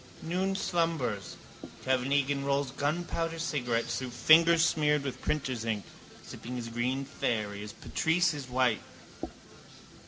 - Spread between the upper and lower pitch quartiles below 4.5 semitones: No, average, 4.9 semitones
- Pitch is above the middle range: No, medium, 140 Hz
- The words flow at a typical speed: No, slow, 125 wpm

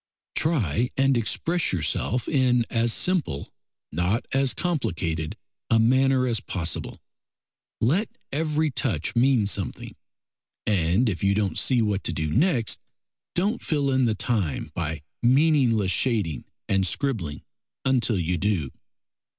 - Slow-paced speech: Yes, slow, 125 wpm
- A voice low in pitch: Yes, low, 115 Hz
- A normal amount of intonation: No, wide, 6.8 semitones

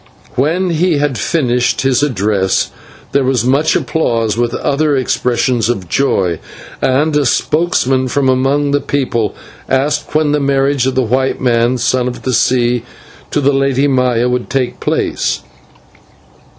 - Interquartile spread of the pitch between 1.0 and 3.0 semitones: Yes, average, 2.7 semitones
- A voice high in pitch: No, low, 130 Hz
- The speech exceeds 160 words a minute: No, average, 150 wpm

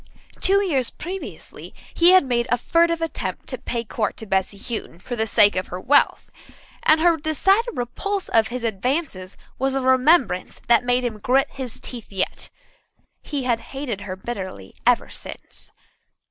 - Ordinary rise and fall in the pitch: No, wide, 6.3 semitones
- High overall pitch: Yes, very high, 250 Hz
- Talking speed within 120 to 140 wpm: No, average, 165 wpm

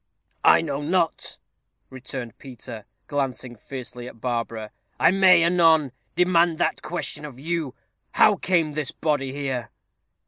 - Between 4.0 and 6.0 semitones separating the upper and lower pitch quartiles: Yes, average, 4.9 semitones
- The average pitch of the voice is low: No, medium, 145 Hz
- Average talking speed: No, slow, 130 wpm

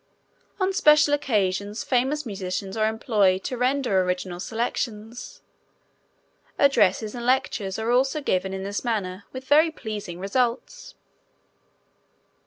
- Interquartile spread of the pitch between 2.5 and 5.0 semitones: No, wide, 5.4 semitones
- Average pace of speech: No, slow, 115 wpm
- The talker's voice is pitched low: No, high, 220 Hz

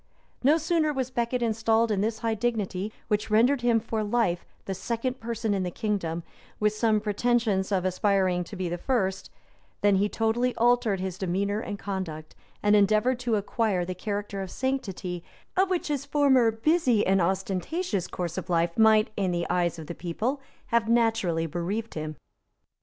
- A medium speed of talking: Yes, average, 175 wpm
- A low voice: No, high, 210 Hz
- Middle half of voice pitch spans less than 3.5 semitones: No, average, 4.0 semitones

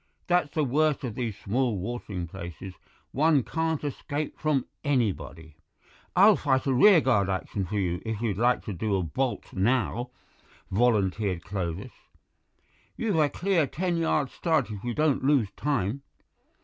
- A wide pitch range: Yes, wide, 7.0 semitones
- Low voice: Yes, low, 125 Hz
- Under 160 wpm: Yes, average, 150 wpm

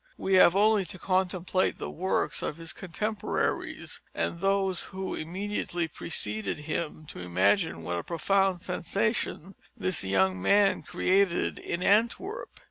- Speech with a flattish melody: No, average, 3.8 semitones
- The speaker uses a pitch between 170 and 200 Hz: Yes, medium, 185 Hz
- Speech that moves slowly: Yes, slow, 130 wpm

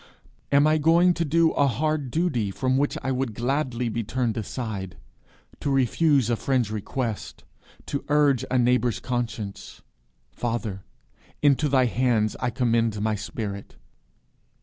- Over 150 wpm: No, average, 140 wpm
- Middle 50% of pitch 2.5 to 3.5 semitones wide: No, average, 3.9 semitones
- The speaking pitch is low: Yes, low, 125 Hz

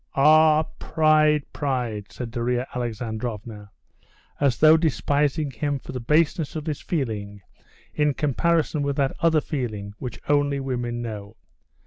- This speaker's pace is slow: Yes, slow, 130 wpm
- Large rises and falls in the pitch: No, average, 4.3 semitones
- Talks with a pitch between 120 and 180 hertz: Yes, low, 135 Hz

